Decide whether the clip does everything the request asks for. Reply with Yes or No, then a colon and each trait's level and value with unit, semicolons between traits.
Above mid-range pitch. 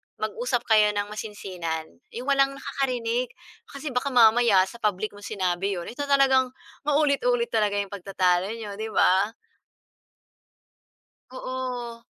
Yes: high, 225 Hz